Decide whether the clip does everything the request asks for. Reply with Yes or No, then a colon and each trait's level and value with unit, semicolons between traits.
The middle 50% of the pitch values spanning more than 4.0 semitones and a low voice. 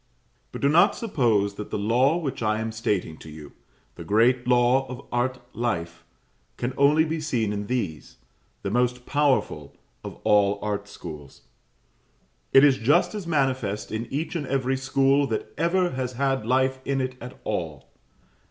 Yes: average, 4.6 semitones; low, 125 Hz